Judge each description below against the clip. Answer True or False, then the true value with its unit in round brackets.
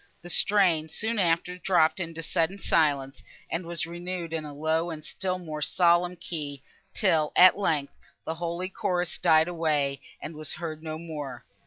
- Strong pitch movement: False (2.4 semitones)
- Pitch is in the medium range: True (165 Hz)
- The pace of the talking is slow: False (165 wpm)